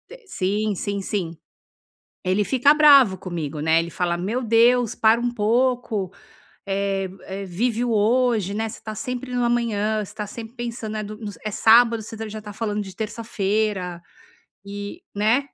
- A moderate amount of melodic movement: Yes, average, 3.1 semitones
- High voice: Yes, high, 215 Hz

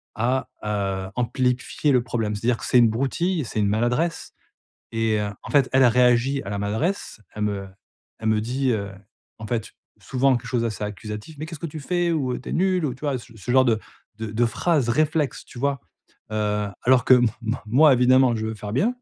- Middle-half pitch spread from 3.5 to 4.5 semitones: Yes, average, 4.0 semitones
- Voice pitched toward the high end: No, low, 120 Hz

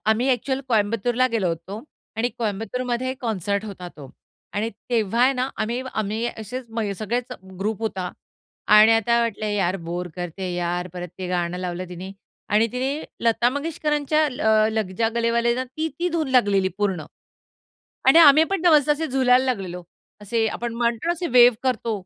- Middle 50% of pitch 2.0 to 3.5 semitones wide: No, average, 4.4 semitones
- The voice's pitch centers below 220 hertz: No, high, 225 Hz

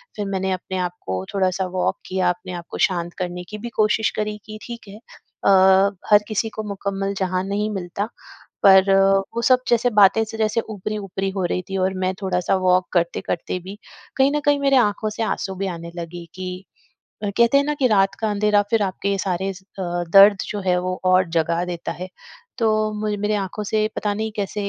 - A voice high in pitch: Yes, high, 195 Hz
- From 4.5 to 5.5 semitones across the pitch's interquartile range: No, narrow, 2.6 semitones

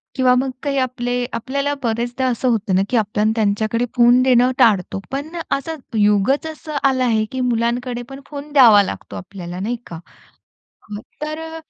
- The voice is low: No, high, 245 Hz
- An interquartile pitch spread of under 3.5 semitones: No, average, 3.8 semitones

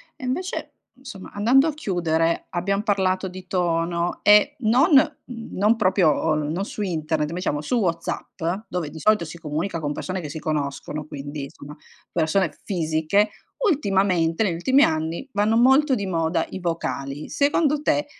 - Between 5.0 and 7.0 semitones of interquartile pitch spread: Yes, average, 5.3 semitones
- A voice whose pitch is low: No, medium, 180 Hz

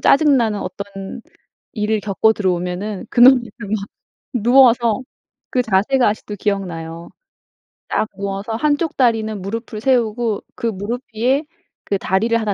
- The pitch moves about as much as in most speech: Yes, average, 3.3 semitones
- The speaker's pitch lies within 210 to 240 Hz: Yes, high, 215 Hz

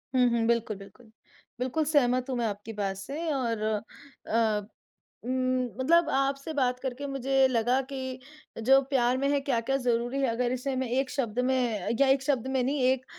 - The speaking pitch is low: No, very high, 255 Hz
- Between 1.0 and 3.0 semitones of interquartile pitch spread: Yes, narrow, 2.4 semitones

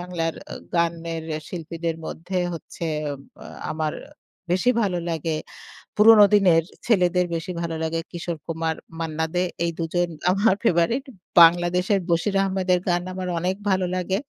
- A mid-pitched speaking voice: Yes, medium, 175 Hz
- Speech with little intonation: Yes, narrow, 2.1 semitones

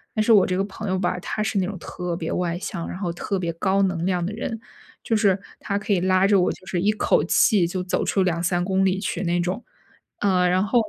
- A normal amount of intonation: No, narrow, 2.1 semitones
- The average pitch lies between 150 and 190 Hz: Yes, medium, 185 Hz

